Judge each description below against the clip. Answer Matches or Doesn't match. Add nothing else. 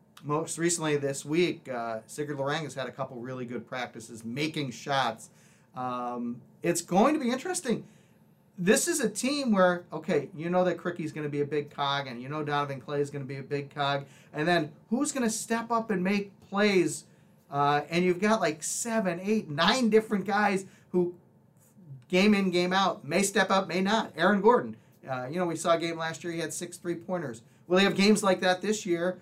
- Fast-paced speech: Matches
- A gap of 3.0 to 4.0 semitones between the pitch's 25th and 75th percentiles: Doesn't match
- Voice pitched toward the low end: Doesn't match